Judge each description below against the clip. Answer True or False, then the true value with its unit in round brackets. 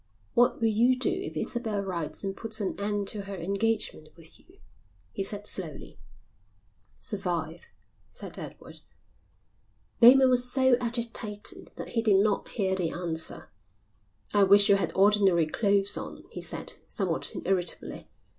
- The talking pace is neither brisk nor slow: True (145 wpm)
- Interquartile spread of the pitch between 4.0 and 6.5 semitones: False (3.2 semitones)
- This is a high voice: True (205 Hz)